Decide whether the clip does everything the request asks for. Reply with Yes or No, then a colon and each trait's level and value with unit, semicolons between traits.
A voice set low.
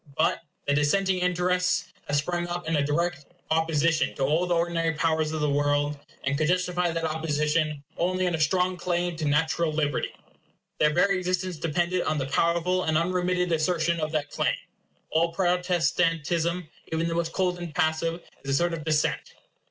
No: medium, 165 Hz